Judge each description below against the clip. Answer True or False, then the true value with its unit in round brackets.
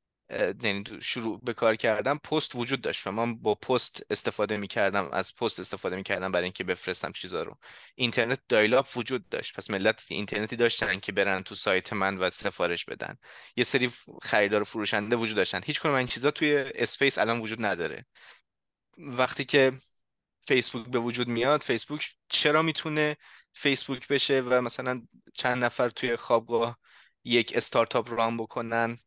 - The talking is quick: True (160 wpm)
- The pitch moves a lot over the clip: False (3.7 semitones)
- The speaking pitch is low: True (120 Hz)